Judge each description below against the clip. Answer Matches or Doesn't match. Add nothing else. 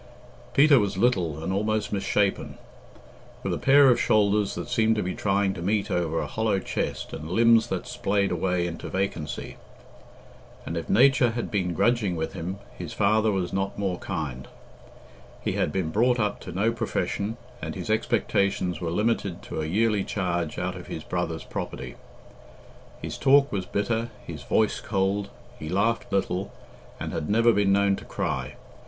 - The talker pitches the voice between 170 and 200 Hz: Doesn't match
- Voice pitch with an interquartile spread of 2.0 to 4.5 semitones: Matches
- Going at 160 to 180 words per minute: Matches